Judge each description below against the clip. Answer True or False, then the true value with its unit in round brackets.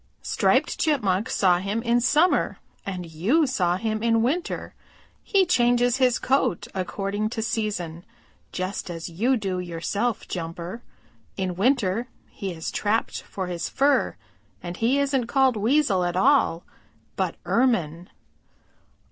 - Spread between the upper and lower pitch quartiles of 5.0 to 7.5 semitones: True (5.6 semitones)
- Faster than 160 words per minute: False (135 wpm)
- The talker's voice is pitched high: True (215 Hz)